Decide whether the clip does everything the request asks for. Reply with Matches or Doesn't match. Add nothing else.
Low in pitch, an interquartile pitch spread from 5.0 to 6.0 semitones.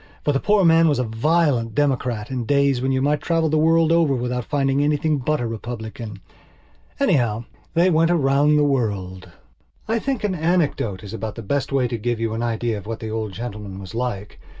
Matches